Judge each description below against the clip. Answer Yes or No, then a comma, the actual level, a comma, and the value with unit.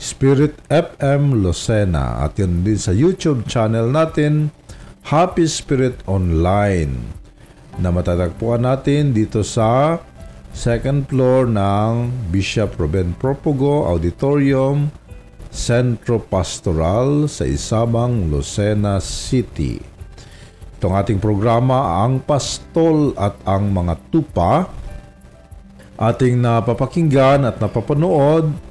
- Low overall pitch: Yes, low, 115 Hz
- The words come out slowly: Yes, slow, 90 wpm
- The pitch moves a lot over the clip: Yes, wide, 6.3 semitones